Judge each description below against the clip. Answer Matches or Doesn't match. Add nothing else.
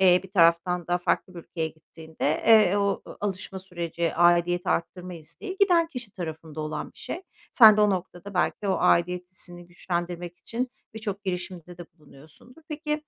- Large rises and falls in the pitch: Doesn't match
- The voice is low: Doesn't match